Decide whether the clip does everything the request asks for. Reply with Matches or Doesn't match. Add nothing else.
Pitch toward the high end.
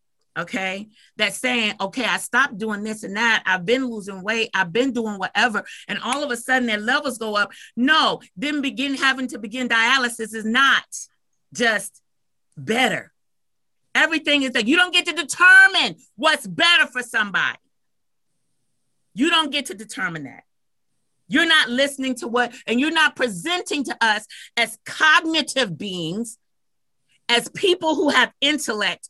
Matches